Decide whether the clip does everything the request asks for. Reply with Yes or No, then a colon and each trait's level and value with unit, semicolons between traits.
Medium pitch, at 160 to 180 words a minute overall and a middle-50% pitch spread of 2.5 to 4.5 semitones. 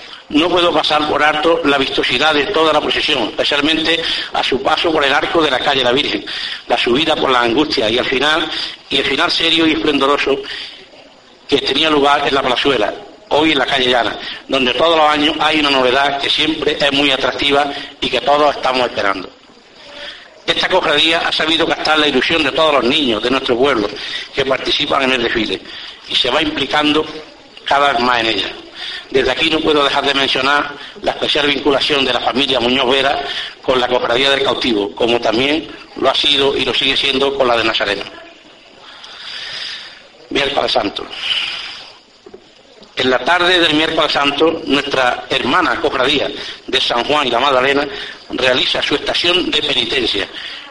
Yes: medium, 145 Hz; average, 175 wpm; average, 2.8 semitones